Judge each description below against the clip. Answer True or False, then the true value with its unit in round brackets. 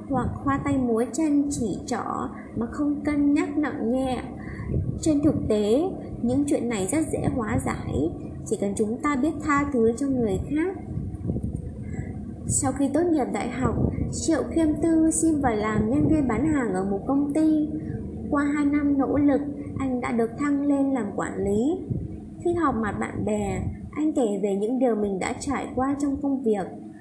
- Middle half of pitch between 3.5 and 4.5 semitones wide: True (4.1 semitones)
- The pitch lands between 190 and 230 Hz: False (275 Hz)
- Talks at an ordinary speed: True (185 wpm)